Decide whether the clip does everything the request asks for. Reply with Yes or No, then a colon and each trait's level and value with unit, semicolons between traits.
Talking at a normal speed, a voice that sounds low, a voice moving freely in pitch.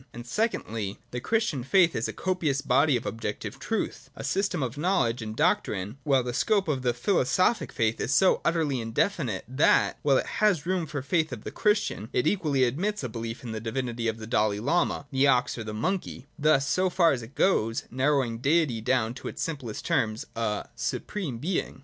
No: fast, 210 wpm; low, 130 Hz; wide, 6.6 semitones